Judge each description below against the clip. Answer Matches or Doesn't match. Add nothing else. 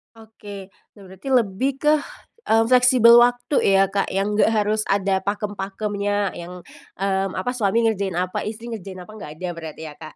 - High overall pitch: Matches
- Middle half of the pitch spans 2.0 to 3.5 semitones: Matches